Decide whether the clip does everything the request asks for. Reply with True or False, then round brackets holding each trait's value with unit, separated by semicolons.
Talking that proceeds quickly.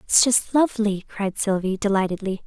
False (145 wpm)